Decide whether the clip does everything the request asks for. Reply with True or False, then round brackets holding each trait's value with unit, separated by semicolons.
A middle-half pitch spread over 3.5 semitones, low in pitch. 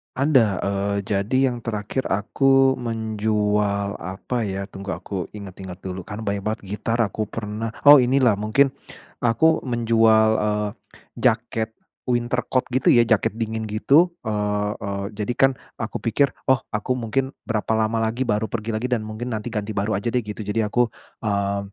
False (2.7 semitones; 110 Hz)